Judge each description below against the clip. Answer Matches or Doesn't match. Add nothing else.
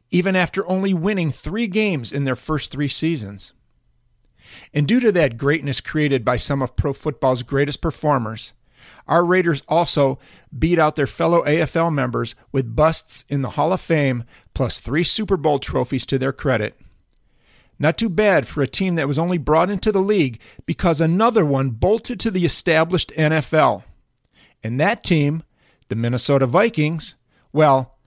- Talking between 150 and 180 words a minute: Matches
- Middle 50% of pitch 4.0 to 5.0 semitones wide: Matches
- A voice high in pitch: Doesn't match